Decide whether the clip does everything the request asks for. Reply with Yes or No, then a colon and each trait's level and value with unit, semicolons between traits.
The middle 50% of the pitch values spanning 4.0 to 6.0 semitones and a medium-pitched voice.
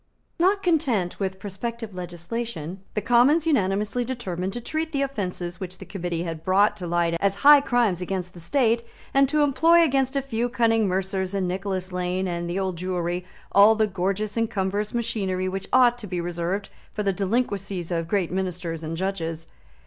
No: average, 4.7 semitones; high, 195 Hz